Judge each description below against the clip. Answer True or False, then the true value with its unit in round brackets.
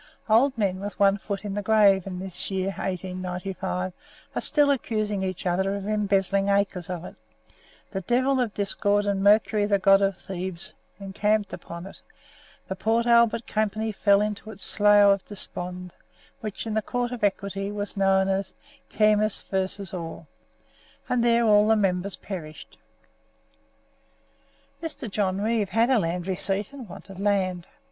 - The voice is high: True (200 Hz)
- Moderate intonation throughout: False (2.1 semitones)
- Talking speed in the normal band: True (155 wpm)